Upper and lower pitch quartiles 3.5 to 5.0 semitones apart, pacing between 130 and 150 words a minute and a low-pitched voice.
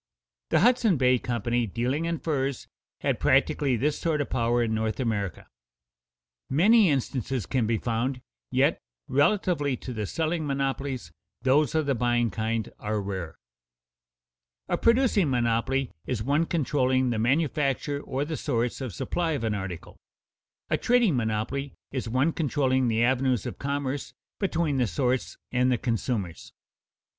Yes: average, 4.0 semitones; average, 145 wpm; low, 130 Hz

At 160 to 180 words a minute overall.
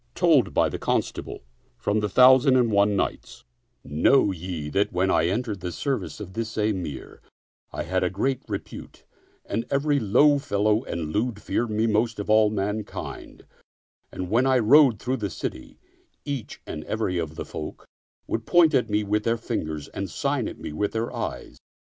Yes: average, 170 wpm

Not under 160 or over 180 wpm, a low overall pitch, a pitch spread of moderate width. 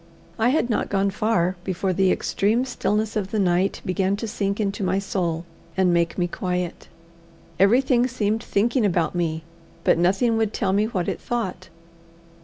No: average, 170 wpm; high, 195 Hz; average, 3.4 semitones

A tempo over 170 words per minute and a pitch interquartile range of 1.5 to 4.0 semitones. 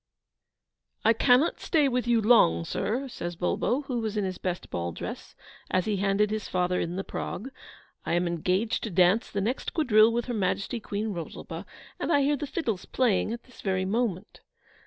No: average, 190 wpm; average, 4.7 semitones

